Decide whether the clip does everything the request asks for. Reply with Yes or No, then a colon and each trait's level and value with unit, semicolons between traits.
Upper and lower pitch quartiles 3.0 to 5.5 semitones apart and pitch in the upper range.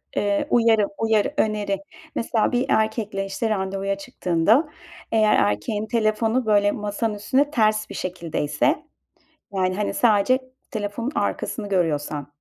No: narrow, 2.4 semitones; high, 210 Hz